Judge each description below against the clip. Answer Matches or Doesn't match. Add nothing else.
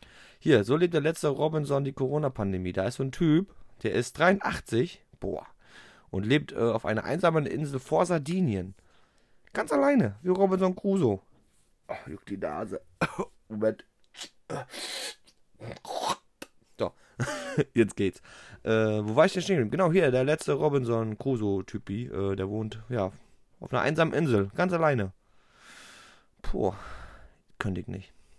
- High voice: Doesn't match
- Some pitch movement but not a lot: Doesn't match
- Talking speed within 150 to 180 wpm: Doesn't match